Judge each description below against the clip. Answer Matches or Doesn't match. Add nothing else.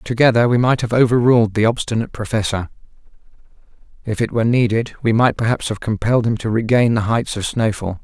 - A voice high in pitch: Doesn't match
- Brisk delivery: Doesn't match